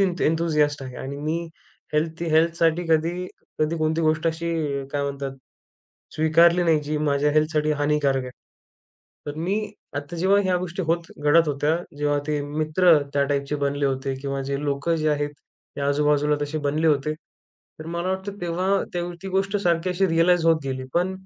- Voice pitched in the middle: Yes, medium, 155 Hz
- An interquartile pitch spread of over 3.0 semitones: No, average, 2.7 semitones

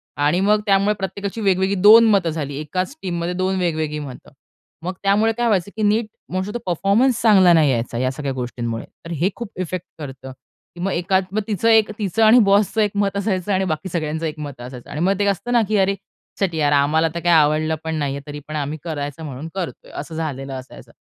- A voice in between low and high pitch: Yes, medium, 175 Hz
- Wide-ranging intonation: No, average, 5.0 semitones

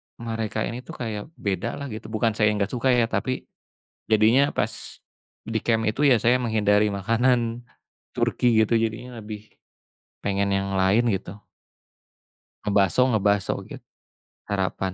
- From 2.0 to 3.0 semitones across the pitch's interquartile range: Yes, narrow, 2.5 semitones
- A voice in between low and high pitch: No, low, 110 Hz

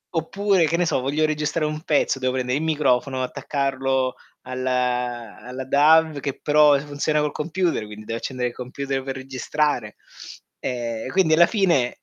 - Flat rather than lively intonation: No, average, 3.4 semitones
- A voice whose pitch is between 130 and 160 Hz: Yes, low, 135 Hz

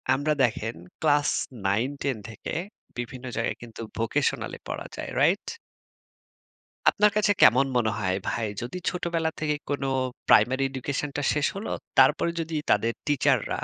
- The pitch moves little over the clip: No, average, 4.5 semitones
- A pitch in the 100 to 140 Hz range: Yes, low, 135 Hz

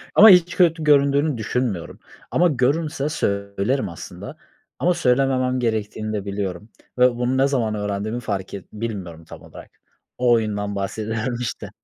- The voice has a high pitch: No, low, 115 Hz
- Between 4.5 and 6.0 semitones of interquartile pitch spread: Yes, average, 5.0 semitones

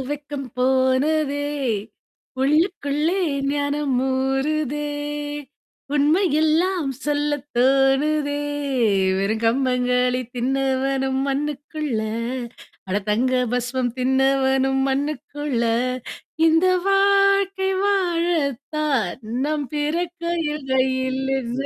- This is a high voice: Yes, very high, 285 Hz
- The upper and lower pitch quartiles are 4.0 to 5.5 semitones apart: No, average, 2.7 semitones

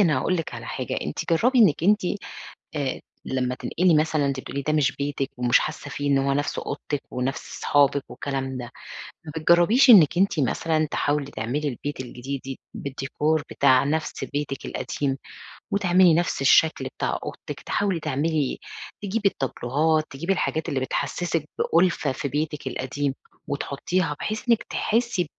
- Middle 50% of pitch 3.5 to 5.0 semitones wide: Yes, average, 3.8 semitones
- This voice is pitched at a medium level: Yes, medium, 145 Hz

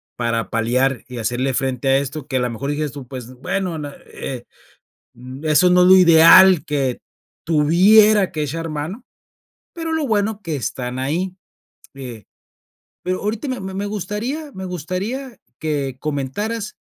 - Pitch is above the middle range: No, medium, 155 Hz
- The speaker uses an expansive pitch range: Yes, wide, 6.8 semitones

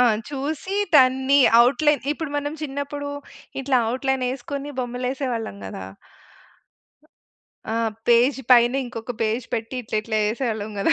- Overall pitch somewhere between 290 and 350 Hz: No, very high, 255 Hz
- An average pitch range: Yes, average, 3.0 semitones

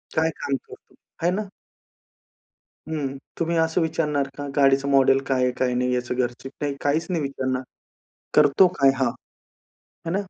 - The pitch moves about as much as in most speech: Yes, average, 3.6 semitones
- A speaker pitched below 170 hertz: Yes, medium, 140 Hz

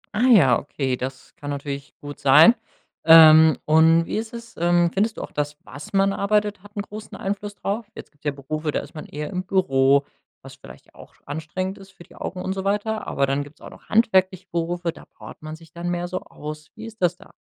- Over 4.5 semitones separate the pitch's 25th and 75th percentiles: Yes, average, 5.0 semitones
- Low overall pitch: No, medium, 170 Hz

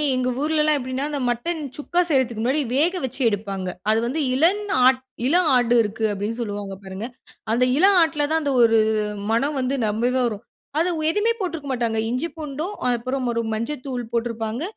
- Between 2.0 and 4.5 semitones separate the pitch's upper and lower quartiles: No, average, 4.9 semitones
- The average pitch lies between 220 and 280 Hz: Yes, very high, 255 Hz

